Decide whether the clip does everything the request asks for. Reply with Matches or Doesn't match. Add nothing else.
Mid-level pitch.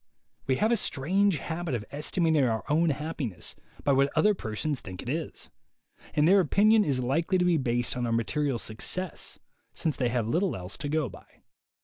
Matches